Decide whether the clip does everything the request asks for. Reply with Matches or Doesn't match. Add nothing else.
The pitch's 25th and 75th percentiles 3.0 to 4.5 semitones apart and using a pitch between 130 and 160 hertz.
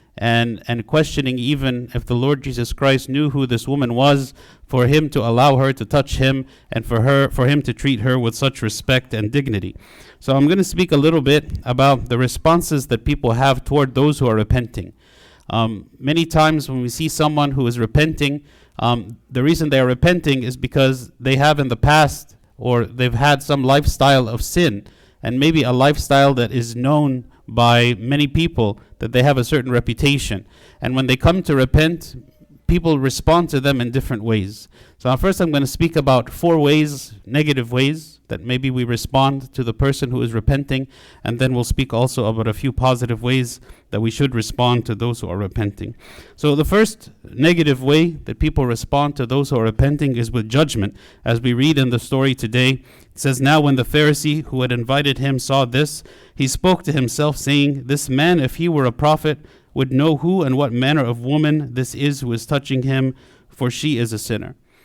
Matches